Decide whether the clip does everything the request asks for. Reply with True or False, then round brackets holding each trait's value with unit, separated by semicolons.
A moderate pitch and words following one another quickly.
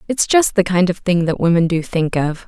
True (180 Hz; 265 wpm)